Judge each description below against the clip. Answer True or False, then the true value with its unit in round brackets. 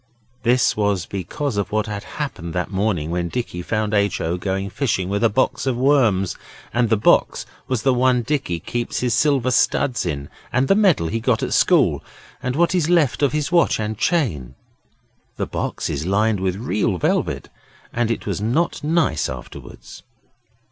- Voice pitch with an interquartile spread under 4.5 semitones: False (5.6 semitones)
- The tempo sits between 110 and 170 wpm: False (180 wpm)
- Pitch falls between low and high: False (110 Hz)